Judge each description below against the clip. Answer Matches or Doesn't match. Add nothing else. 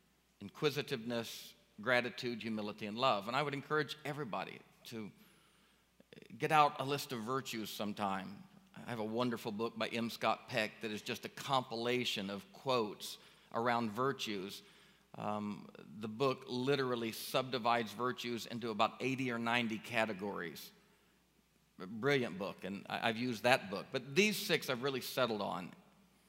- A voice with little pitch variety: Doesn't match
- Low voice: Matches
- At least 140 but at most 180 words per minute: Matches